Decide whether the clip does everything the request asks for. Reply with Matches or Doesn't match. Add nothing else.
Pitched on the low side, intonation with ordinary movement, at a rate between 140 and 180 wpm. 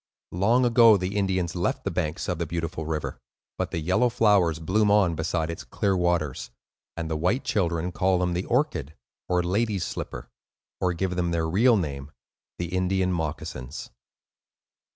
Matches